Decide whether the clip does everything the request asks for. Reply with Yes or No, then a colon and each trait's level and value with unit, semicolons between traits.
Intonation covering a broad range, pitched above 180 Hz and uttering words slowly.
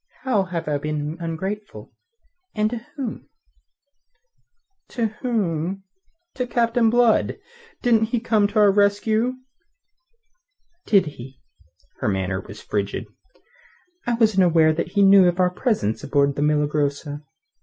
Yes: wide, 6.8 semitones; high, 190 Hz; slow, 125 wpm